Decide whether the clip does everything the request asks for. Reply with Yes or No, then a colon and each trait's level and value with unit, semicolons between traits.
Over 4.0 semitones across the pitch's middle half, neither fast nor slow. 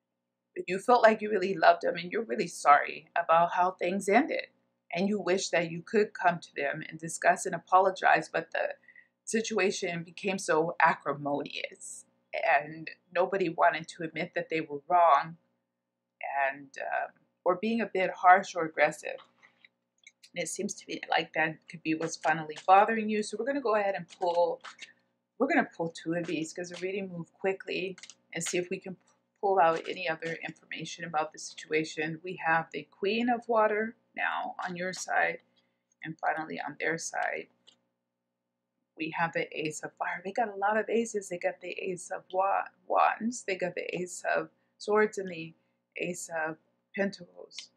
No: average, 3.7 semitones; average, 180 wpm